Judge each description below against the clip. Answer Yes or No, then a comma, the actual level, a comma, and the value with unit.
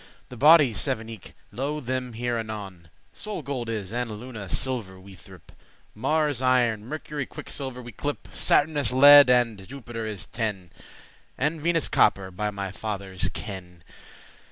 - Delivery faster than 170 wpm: No, average, 155 wpm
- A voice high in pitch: No, low, 120 Hz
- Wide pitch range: No, average, 5.0 semitones